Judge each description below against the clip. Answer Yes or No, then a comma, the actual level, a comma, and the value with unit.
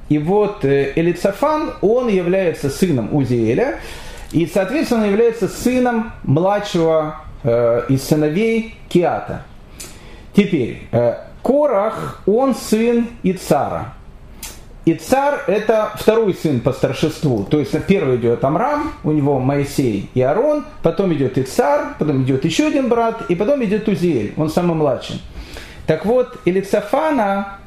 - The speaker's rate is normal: Yes, average, 125 wpm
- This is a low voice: No, medium, 185 Hz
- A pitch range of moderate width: No, wide, 7.5 semitones